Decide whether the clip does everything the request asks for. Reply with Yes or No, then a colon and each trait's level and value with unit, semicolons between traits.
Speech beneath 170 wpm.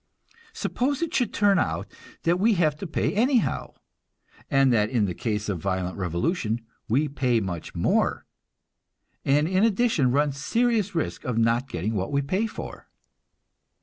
Yes: average, 155 wpm